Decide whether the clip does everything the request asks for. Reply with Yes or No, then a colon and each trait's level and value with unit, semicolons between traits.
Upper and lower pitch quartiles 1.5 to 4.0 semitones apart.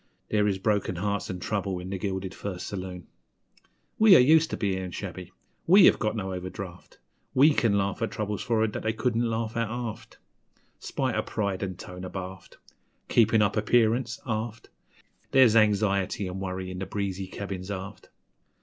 Yes: average, 3.1 semitones